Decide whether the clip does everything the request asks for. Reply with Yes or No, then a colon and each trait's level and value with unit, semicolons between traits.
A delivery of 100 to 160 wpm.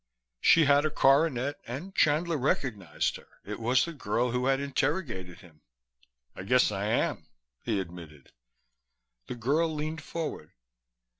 Yes: average, 140 wpm